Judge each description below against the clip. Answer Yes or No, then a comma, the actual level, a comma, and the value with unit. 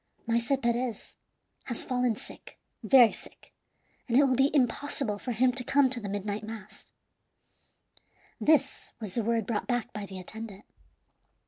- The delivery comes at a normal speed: Yes, average, 150 wpm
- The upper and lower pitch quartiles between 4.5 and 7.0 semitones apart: No, average, 3.2 semitones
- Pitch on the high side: Yes, high, 235 Hz